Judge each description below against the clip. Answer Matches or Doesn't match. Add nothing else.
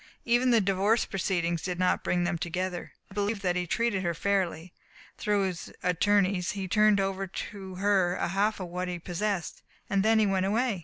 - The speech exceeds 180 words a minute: Matches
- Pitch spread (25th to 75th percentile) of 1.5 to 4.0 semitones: Matches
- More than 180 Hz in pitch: Matches